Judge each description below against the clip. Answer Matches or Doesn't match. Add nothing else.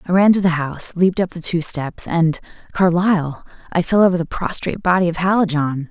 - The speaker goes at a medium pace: Matches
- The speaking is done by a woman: Matches